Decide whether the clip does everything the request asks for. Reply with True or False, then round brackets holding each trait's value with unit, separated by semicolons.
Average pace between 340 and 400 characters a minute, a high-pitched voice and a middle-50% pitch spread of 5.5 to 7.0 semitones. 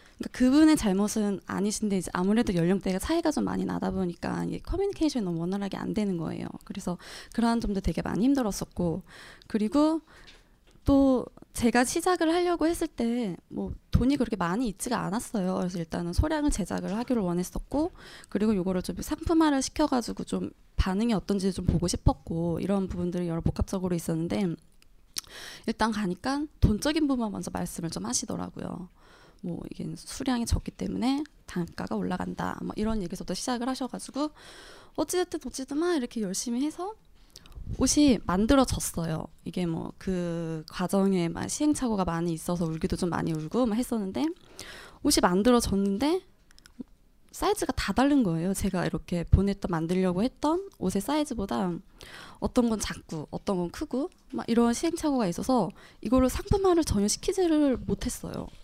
True (360 characters per minute; 215 Hz; 6.7 semitones)